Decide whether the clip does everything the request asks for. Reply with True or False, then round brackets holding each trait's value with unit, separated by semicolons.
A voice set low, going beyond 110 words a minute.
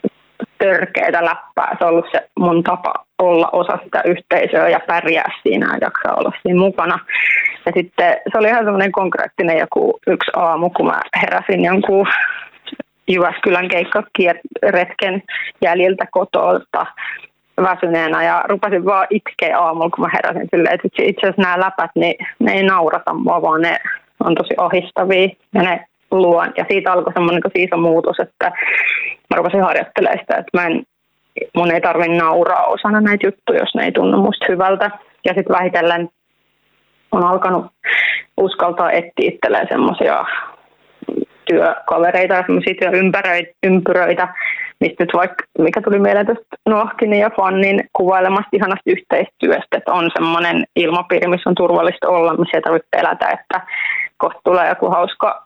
False (185 Hz; 145 wpm)